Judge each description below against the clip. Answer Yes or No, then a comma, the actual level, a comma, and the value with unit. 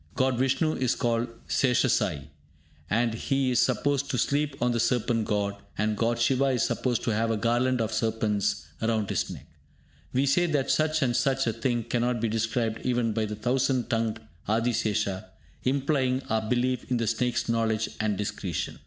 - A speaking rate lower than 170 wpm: No, average, 175 wpm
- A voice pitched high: No, low, 120 Hz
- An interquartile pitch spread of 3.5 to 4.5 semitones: No, average, 2.7 semitones